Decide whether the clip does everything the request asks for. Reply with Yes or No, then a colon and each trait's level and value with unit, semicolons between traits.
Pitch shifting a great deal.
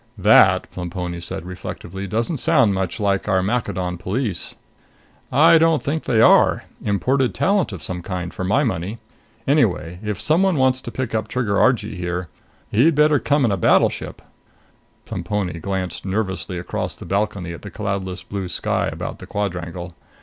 Yes: wide, 5.7 semitones